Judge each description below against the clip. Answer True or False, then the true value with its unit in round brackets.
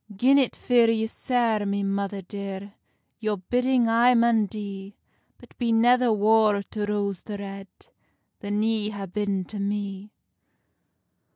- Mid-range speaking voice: False (210 Hz)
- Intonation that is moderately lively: False (2.3 semitones)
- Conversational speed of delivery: True (145 wpm)